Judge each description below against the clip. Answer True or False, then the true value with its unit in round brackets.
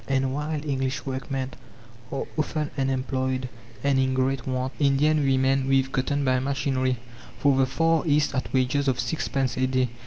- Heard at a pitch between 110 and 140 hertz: True (135 Hz)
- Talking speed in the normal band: True (165 wpm)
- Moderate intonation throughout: False (1.4 semitones)